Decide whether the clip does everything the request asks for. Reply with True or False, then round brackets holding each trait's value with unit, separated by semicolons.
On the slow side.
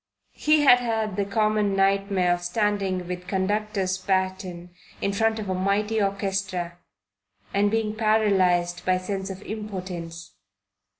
True (130 wpm)